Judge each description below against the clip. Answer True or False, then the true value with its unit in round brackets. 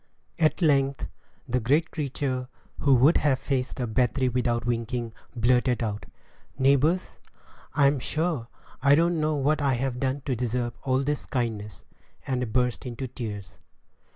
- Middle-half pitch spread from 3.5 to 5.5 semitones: False (2.7 semitones)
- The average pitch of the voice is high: False (130 Hz)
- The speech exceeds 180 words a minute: False (145 wpm)